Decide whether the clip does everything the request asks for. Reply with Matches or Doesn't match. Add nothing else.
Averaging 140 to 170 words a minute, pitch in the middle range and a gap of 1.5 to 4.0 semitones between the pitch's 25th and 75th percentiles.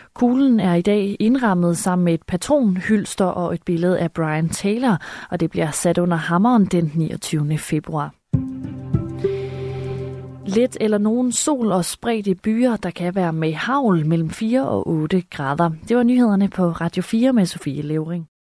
Doesn't match